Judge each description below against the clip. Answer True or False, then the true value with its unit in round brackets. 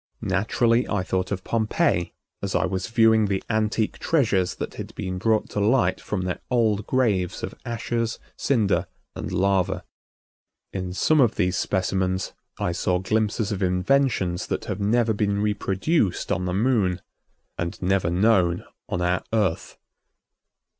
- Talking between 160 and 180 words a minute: False (145 wpm)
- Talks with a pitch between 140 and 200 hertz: False (100 Hz)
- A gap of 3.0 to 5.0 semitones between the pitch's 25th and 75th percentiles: True (3.5 semitones)